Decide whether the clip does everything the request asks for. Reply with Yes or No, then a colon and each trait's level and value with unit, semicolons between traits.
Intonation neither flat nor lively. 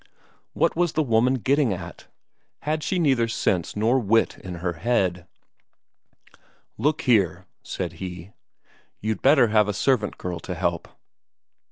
No: wide, 6.4 semitones